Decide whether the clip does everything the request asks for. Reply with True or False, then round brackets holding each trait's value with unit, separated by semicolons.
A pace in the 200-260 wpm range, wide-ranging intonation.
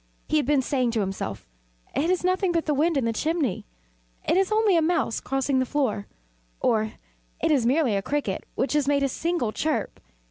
True (205 wpm; 5.7 semitones)